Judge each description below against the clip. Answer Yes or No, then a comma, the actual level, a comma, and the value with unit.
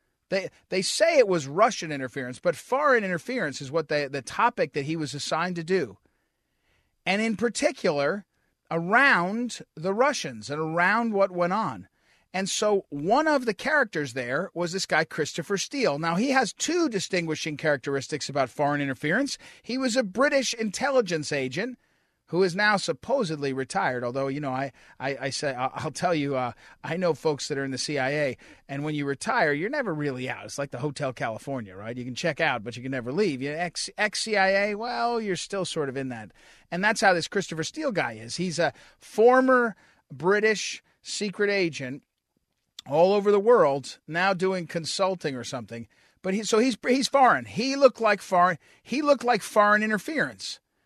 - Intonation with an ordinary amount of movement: No, wide, 7.1 semitones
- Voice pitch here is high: No, medium, 175 Hz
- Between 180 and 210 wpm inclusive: Yes, average, 185 wpm